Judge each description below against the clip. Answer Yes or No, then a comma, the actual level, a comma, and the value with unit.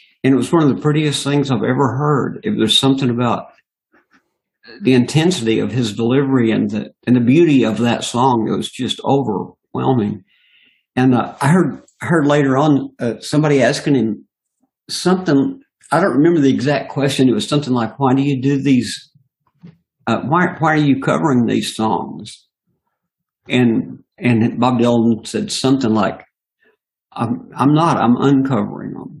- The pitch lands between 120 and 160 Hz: Yes, low, 135 Hz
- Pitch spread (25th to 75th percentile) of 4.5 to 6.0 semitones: No, average, 3.7 semitones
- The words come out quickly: No, average, 165 wpm